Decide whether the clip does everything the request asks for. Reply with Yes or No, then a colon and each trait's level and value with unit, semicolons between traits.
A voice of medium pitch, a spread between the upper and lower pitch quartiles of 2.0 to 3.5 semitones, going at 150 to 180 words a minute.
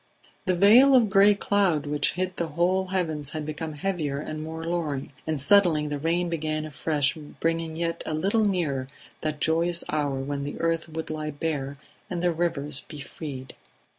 Yes: medium, 160 Hz; average, 2.8 semitones; average, 175 wpm